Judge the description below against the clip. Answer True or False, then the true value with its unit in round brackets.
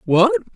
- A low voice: False (185 Hz)